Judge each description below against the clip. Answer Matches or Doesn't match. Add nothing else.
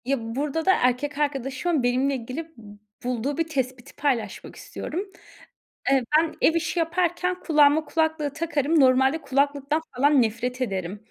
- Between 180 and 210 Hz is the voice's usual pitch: Doesn't match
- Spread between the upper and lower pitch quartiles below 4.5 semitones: Matches